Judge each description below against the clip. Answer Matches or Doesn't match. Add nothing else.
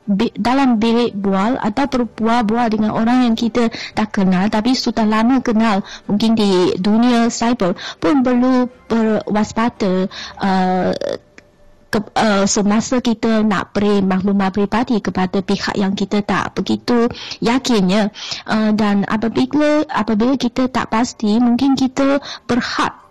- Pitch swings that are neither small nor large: Matches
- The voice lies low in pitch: Doesn't match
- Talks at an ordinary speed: Matches